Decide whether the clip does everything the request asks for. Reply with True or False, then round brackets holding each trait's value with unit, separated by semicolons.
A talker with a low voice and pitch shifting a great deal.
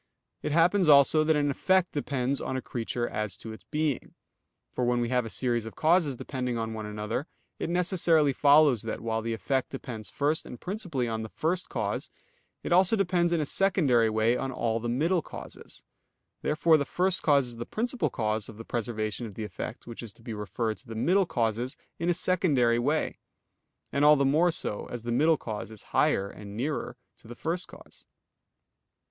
True (130 Hz; 5.8 semitones)